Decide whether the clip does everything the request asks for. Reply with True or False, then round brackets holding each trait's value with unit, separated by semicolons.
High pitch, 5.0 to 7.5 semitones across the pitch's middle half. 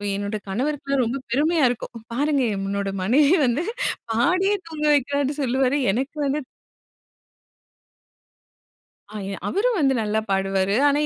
True (265 Hz; 5.5 semitones)